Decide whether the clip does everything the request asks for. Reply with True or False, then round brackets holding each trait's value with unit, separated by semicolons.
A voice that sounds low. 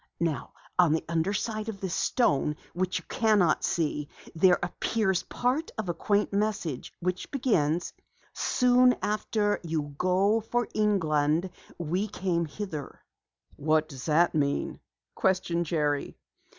False (180 Hz)